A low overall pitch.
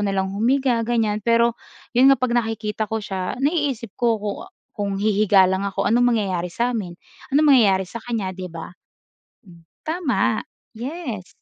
No: high, 220 Hz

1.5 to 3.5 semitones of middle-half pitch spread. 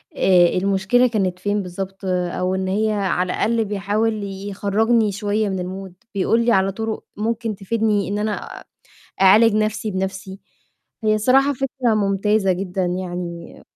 Yes: narrow, 2.4 semitones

